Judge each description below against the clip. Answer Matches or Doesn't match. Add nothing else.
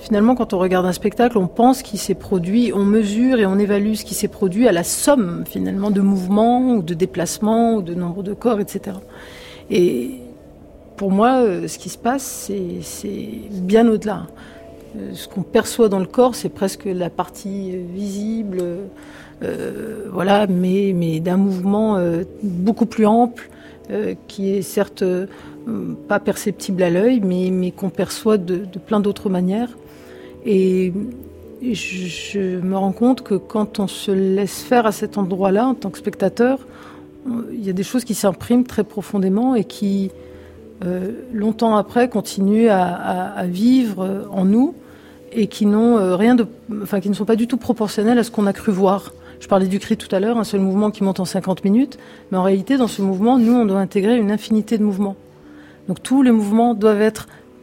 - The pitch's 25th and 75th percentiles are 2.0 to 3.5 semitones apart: Matches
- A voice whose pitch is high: Matches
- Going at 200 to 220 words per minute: Doesn't match